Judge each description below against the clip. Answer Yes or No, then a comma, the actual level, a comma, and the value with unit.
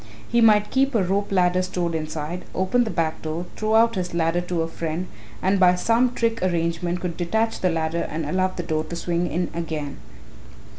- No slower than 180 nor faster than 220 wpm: Yes, average, 200 wpm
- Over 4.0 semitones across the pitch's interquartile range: No, average, 3.1 semitones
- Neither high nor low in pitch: Yes, medium, 180 Hz